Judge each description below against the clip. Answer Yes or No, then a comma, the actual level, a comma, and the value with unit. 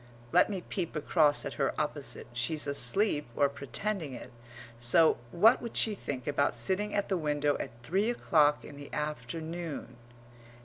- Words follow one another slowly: No, average, 160 wpm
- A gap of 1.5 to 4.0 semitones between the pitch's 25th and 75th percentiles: No, average, 4.9 semitones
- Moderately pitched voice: Yes, medium, 150 Hz